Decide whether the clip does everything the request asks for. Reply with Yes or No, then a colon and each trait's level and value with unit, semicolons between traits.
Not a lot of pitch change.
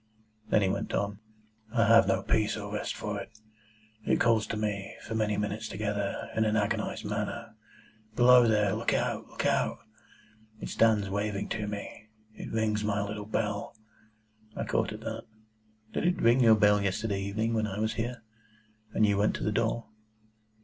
Yes: narrow, 1.6 semitones